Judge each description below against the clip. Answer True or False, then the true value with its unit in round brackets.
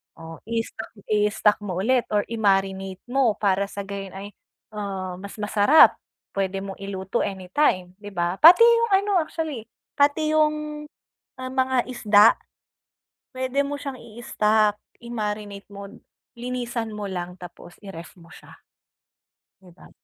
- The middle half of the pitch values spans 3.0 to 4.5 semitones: False (4.9 semitones)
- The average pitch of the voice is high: True (210 Hz)